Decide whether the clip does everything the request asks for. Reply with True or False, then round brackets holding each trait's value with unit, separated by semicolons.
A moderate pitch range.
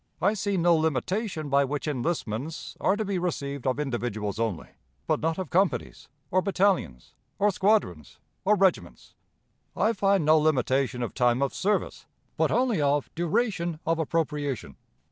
False (5.9 semitones)